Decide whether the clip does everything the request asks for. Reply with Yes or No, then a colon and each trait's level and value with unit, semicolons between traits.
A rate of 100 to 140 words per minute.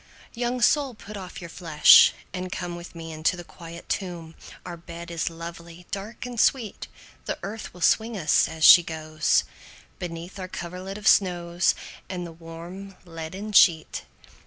No: average, 165 wpm